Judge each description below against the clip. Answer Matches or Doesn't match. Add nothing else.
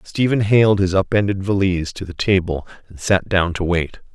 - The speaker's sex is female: Doesn't match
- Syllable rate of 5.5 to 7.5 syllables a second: Doesn't match